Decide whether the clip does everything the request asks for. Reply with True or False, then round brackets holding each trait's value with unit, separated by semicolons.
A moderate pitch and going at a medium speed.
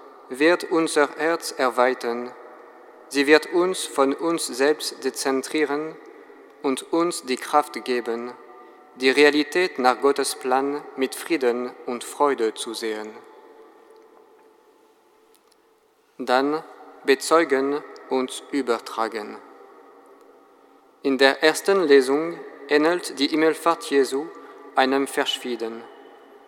False (150 Hz; 95 wpm)